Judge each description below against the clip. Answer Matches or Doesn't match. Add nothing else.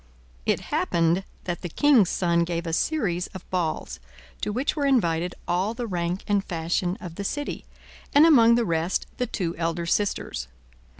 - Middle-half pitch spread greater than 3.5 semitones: Matches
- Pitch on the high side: Doesn't match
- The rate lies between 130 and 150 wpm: Doesn't match